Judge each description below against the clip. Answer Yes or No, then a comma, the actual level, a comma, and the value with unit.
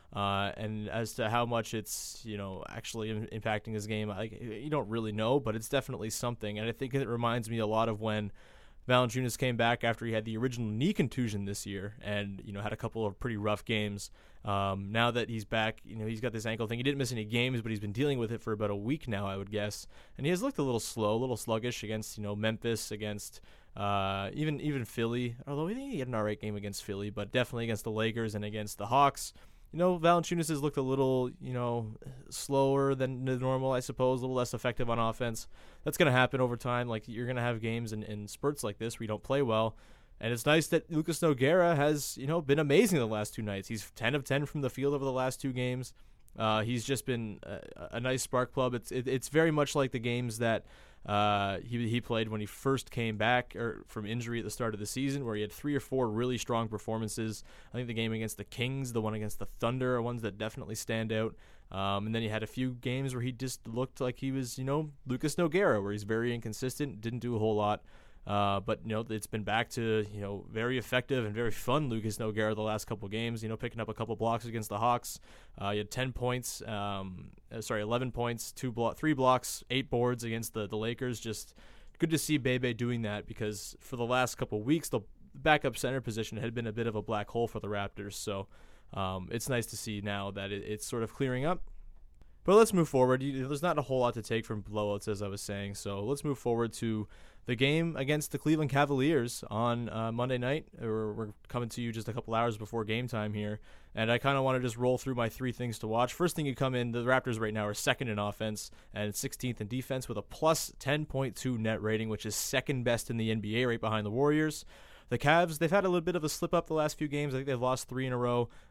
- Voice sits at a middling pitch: No, low, 115 Hz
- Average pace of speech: No, fast, 250 wpm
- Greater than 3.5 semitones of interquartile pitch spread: No, average, 3.2 semitones